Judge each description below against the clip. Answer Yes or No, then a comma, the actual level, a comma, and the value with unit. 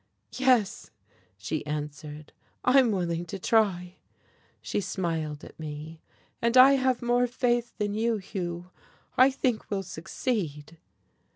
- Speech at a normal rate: No, slow, 120 wpm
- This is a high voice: Yes, high, 195 Hz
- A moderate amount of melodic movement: No, wide, 6.8 semitones